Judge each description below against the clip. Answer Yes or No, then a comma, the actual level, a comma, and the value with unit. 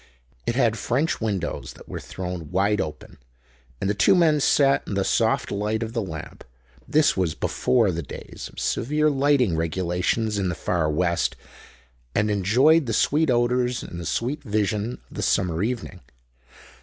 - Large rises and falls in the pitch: Yes, wide, 6.1 semitones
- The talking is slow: No, average, 160 wpm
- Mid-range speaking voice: No, low, 105 Hz